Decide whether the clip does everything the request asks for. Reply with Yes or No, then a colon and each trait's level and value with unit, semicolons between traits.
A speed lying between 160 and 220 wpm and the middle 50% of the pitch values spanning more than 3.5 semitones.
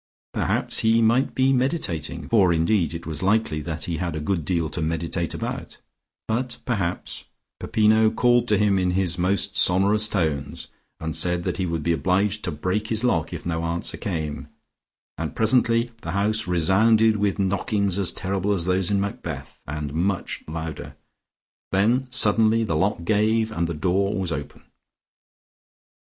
Yes: average, 165 wpm; average, 4.5 semitones